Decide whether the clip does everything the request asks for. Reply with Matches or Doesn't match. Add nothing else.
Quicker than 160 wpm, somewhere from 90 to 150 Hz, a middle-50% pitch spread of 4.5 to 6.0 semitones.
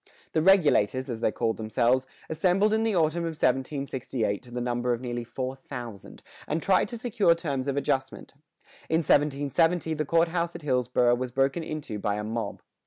Matches